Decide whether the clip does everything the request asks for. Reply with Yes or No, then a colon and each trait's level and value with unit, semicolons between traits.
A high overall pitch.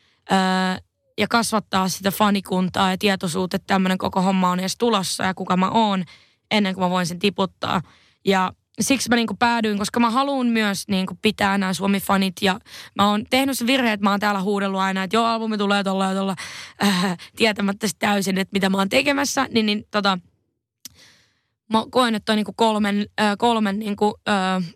Yes: high, 200 Hz